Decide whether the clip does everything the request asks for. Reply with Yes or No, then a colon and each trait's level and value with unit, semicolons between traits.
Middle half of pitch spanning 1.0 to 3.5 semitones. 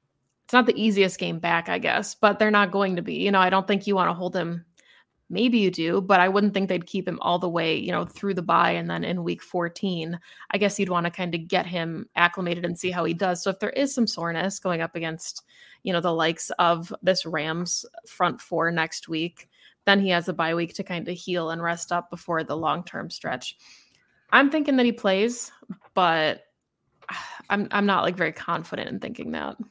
Yes: average, 2.9 semitones